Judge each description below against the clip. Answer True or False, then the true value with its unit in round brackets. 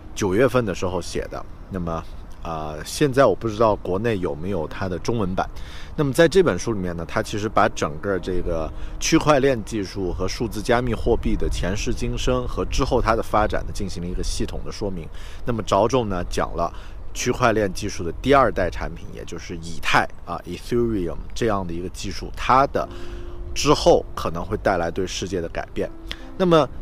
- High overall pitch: False (90 Hz)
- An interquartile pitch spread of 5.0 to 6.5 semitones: True (5.3 semitones)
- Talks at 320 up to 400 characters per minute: False (305 characters per minute)